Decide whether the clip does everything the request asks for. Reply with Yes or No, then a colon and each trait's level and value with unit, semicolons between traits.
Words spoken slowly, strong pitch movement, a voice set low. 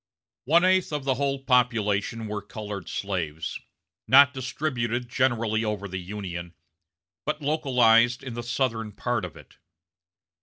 No: slow, 130 wpm; average, 4.3 semitones; low, 120 Hz